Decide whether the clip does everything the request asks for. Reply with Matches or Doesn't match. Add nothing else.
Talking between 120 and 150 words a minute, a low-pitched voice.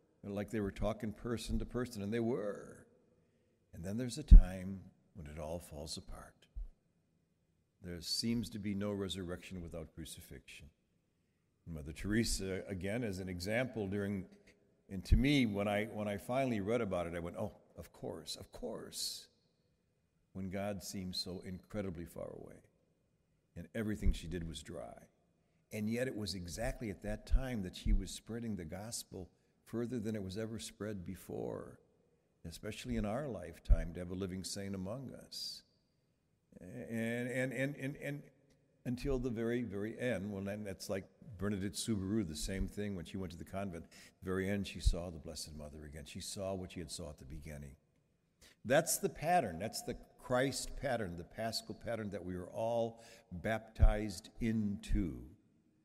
Doesn't match